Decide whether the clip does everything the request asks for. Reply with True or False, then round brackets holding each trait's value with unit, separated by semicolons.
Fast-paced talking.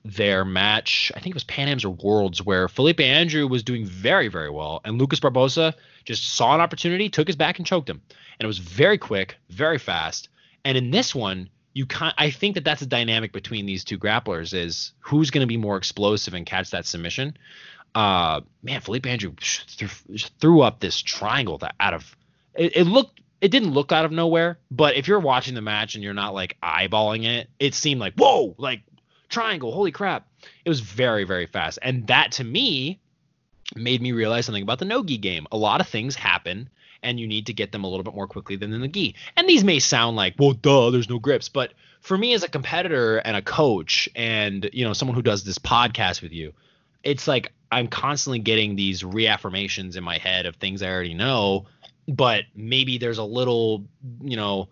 True (210 wpm)